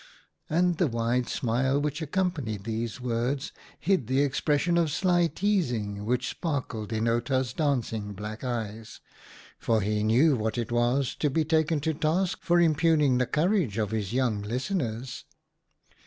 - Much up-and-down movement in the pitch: Yes, wide, 5.8 semitones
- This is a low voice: Yes, low, 130 Hz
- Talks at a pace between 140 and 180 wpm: Yes, average, 155 wpm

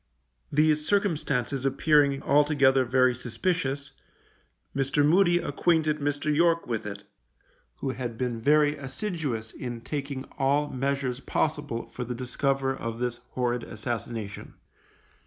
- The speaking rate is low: Yes, slow, 120 wpm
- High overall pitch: No, low, 135 Hz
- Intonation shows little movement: No, average, 3.3 semitones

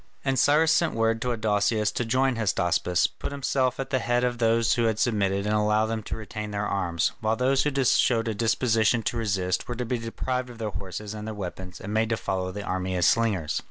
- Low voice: Yes, low, 110 Hz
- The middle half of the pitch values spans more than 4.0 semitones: No, average, 3.2 semitones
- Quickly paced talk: Yes, fast, 230 wpm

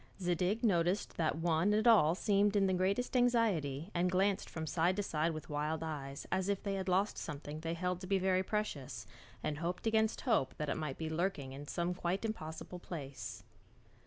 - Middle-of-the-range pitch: Yes, medium, 180 Hz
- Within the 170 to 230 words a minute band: Yes, average, 195 wpm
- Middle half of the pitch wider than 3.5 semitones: Yes, average, 4.0 semitones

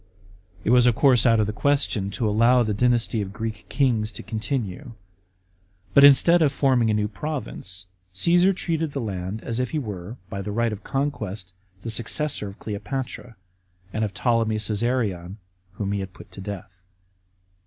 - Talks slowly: No, average, 175 wpm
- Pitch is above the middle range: No, low, 115 Hz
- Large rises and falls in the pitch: No, average, 4.3 semitones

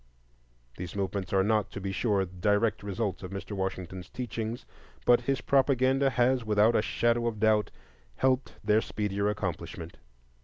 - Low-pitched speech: Yes, low, 105 Hz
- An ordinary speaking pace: Yes, average, 150 wpm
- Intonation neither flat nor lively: Yes, average, 3.5 semitones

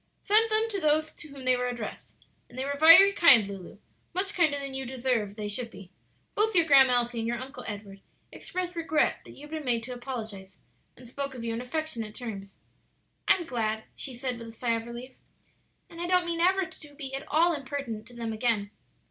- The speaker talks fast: Yes, fast, 215 wpm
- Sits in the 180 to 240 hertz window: No, very high, 255 Hz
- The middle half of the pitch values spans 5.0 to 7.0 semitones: Yes, wide, 5.4 semitones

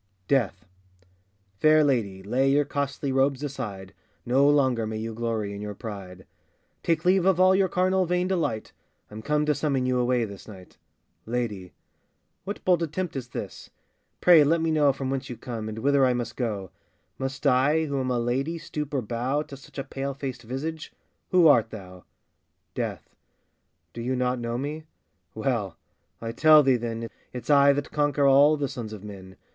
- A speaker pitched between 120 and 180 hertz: Yes, low, 135 Hz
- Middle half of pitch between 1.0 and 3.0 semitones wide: No, average, 4.4 semitones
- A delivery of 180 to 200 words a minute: Yes, average, 185 wpm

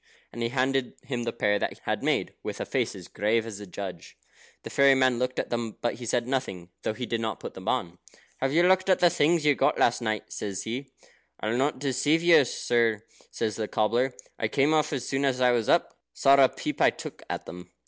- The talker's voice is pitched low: Yes, low, 125 Hz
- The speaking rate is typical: No, fast, 235 wpm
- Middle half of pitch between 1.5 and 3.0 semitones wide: No, average, 3.7 semitones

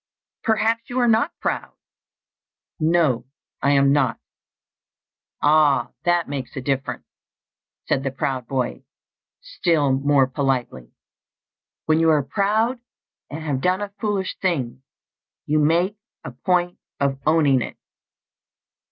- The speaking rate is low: Yes, slow, 120 wpm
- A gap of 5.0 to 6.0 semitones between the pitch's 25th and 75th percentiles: Yes, wide, 5.4 semitones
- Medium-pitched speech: Yes, medium, 150 Hz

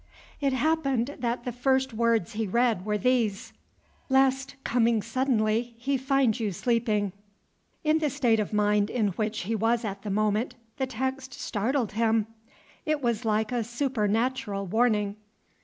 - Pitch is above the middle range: Yes, high, 235 Hz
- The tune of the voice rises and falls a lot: No, average, 3.5 semitones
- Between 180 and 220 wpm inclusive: No, average, 150 wpm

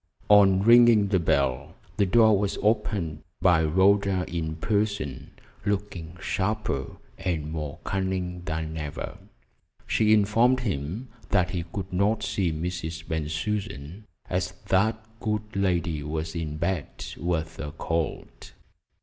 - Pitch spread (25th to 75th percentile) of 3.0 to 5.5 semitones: Yes, average, 4.4 semitones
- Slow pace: Yes, slow, 125 wpm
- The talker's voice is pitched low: Yes, very low, 90 Hz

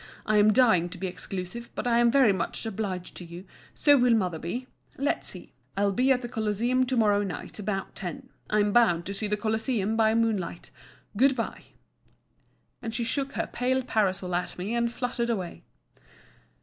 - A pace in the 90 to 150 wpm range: No, average, 180 wpm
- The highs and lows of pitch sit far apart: No, average, 3.9 semitones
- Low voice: No, high, 220 Hz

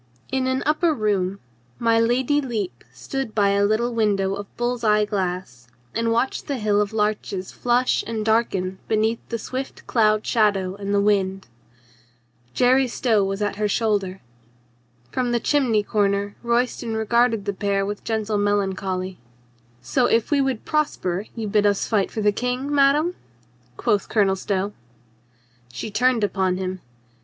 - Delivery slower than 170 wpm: Yes, average, 155 wpm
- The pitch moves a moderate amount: Yes, average, 3.3 semitones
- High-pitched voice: Yes, high, 215 Hz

